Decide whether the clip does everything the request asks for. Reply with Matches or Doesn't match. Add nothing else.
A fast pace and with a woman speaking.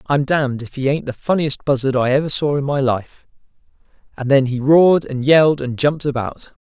Doesn't match